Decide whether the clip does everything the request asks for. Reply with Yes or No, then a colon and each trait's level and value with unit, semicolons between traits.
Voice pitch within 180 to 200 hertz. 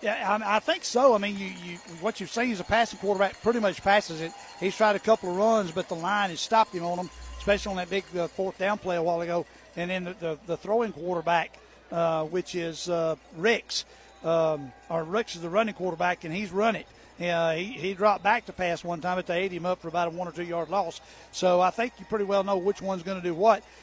Yes: medium, 185 Hz